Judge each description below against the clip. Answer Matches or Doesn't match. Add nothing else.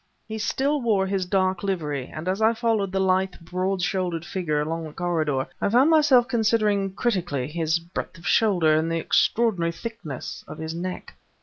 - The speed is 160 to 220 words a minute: Matches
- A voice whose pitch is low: Doesn't match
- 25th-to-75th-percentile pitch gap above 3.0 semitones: Matches